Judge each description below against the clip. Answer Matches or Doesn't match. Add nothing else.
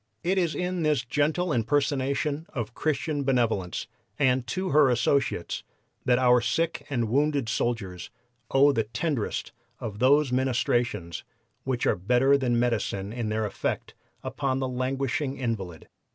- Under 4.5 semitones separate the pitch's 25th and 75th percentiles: Matches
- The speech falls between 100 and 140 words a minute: Matches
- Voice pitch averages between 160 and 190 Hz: Doesn't match